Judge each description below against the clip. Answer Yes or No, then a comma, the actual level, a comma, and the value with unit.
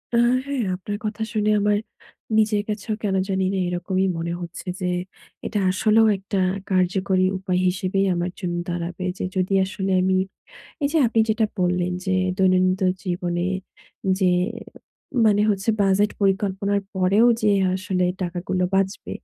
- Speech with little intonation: Yes, narrow, 2.1 semitones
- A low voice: No, high, 190 Hz